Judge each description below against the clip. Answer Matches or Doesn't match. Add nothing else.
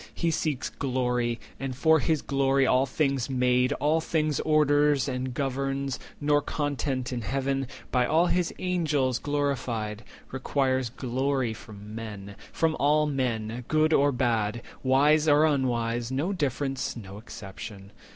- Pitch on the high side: Doesn't match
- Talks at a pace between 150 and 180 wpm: Doesn't match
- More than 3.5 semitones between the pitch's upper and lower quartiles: Doesn't match